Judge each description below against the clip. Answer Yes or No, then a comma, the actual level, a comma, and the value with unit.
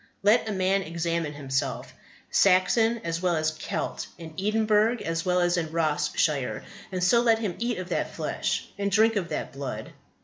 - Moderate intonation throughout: Yes, average, 4.8 semitones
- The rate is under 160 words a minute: No, average, 180 wpm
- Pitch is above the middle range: No, medium, 180 Hz